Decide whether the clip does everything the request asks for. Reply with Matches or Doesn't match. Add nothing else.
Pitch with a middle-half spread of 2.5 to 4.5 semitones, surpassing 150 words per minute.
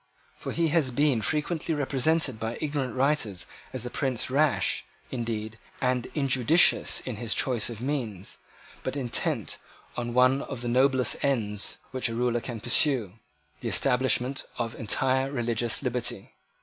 Doesn't match